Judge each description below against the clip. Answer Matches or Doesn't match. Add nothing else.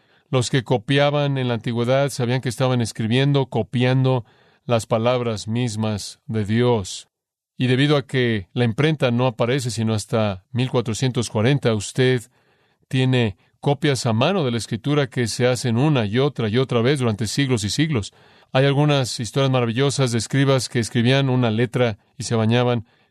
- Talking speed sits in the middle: Matches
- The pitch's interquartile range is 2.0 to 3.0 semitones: Matches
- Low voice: Matches